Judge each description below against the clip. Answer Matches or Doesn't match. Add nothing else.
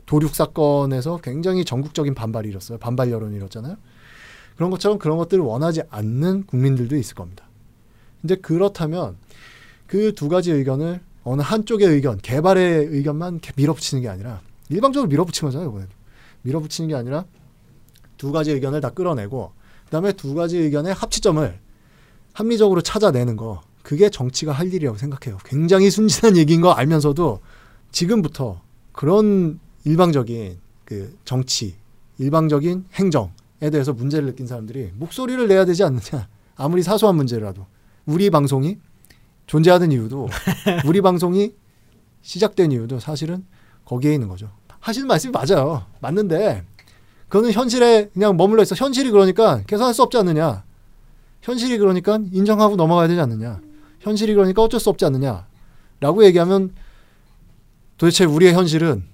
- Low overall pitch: Doesn't match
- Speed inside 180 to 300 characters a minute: Doesn't match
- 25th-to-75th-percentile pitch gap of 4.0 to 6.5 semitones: Doesn't match